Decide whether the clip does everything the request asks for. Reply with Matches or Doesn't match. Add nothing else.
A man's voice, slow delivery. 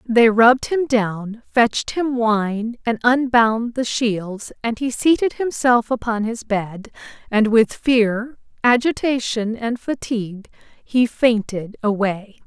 Doesn't match